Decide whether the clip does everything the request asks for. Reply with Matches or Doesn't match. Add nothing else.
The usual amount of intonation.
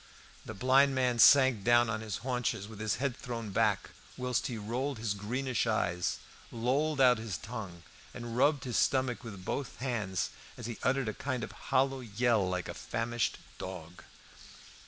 Matches